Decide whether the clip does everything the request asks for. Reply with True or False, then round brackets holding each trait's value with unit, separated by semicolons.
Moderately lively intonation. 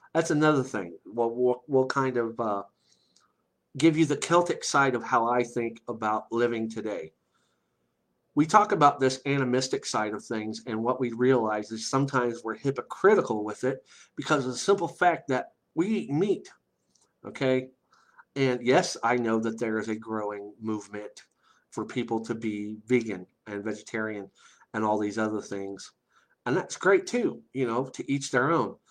True (3.6 semitones)